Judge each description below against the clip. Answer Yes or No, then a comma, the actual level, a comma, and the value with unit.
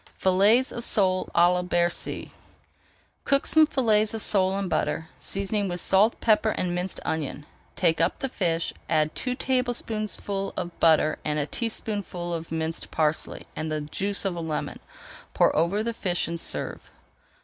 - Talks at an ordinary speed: Yes, average, 160 wpm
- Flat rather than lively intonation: No, average, 4.5 semitones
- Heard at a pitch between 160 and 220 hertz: Yes, medium, 185 Hz